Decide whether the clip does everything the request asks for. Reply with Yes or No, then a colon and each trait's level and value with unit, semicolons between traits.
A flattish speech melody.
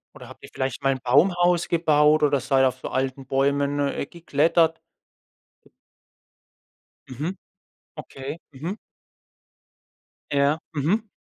No: average, 3.4 semitones